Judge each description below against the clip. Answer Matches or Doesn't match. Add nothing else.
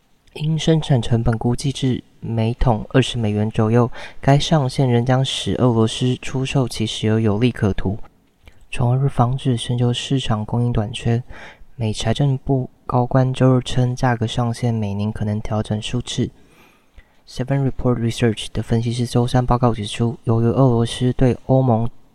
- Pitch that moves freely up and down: Doesn't match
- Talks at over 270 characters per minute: Matches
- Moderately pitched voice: Doesn't match